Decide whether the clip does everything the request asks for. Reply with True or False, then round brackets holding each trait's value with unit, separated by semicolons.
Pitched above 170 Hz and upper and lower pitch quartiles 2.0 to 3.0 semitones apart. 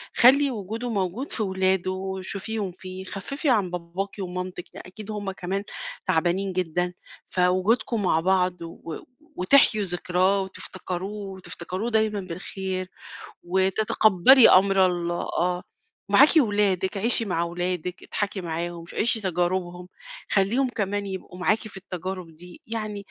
True (190 Hz; 2.4 semitones)